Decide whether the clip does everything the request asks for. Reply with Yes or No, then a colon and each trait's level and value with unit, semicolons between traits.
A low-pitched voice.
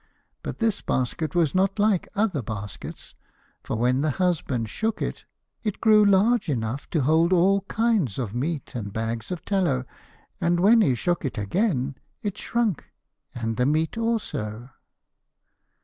No: medium, 160 Hz